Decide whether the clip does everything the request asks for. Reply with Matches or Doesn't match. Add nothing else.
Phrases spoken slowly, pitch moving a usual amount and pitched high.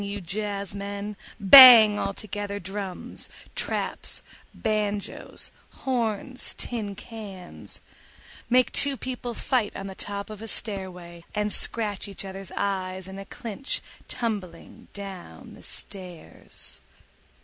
Doesn't match